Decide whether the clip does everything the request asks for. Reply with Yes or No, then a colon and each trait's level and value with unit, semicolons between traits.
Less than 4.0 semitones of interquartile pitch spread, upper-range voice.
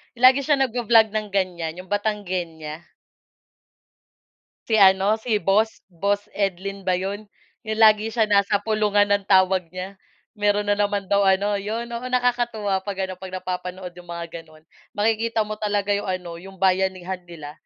Yes: narrow, 2.6 semitones; high, 200 Hz